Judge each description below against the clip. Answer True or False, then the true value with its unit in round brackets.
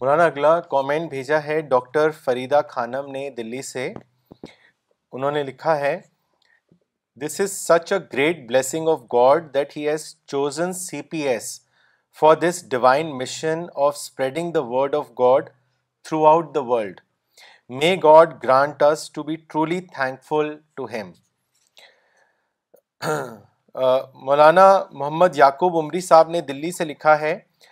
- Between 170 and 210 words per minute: False (140 wpm)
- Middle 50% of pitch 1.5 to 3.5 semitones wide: True (3.1 semitones)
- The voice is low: False (150 Hz)